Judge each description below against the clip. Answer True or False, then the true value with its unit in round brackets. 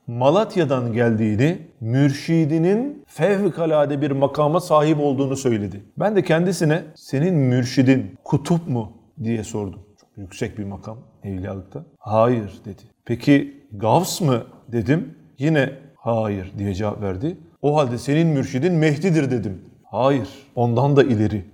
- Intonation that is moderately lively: False (5.8 semitones)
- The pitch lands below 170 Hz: True (135 Hz)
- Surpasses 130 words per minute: False (125 wpm)